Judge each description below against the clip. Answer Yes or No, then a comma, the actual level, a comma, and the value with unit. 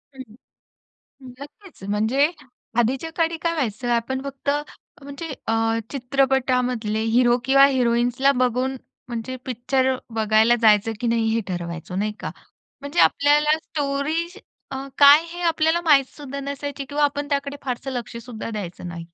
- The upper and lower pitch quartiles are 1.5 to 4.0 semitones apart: Yes, average, 3.6 semitones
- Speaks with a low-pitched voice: No, very high, 265 Hz